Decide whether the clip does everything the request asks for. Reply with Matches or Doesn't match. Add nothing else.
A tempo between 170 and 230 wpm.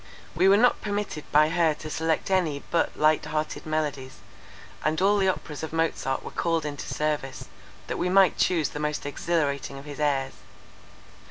Matches